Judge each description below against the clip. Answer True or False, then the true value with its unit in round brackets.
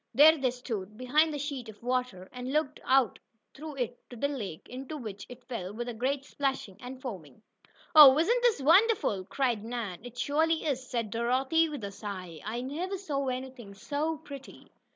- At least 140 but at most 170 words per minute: False (185 wpm)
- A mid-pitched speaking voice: False (255 Hz)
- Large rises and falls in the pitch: False (4.4 semitones)